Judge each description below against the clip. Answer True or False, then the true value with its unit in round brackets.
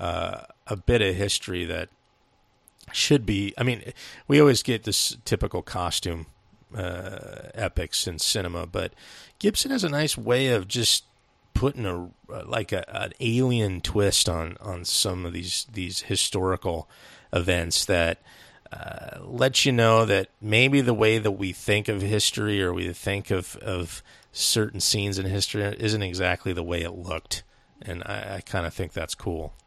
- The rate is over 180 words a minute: False (160 wpm)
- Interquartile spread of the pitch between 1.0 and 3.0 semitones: False (4.0 semitones)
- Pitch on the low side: True (100 Hz)